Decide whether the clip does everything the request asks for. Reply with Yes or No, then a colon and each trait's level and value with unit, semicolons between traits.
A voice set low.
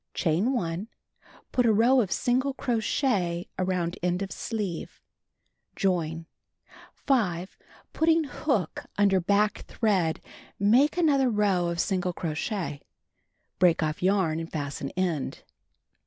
No: high, 190 Hz